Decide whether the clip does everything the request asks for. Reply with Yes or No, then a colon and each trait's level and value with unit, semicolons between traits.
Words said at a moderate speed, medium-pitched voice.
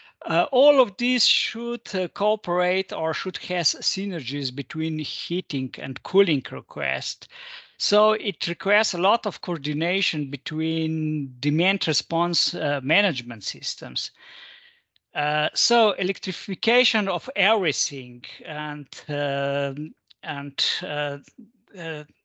No: slow, 105 wpm; medium, 165 Hz